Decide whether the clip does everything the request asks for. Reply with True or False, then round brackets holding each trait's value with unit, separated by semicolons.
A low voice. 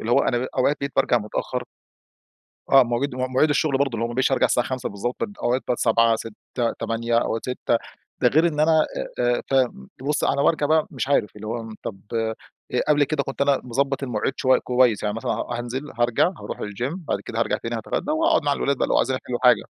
True (125 Hz)